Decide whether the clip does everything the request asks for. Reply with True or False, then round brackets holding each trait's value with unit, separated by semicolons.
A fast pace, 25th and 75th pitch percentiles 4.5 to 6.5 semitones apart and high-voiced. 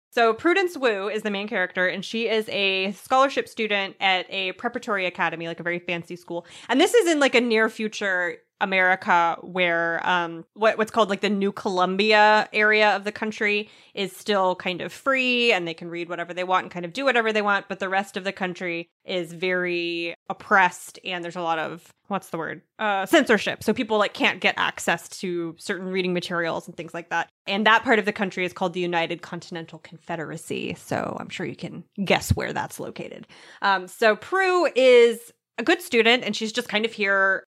False (210 wpm; 3.7 semitones; 195 Hz)